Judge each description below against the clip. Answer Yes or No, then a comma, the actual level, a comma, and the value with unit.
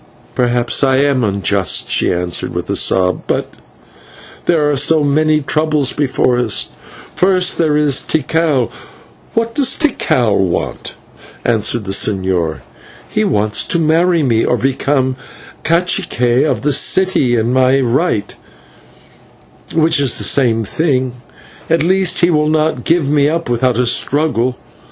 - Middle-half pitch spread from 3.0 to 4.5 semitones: No, average, 4.9 semitones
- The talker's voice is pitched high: No, low, 135 Hz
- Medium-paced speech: Yes, average, 145 wpm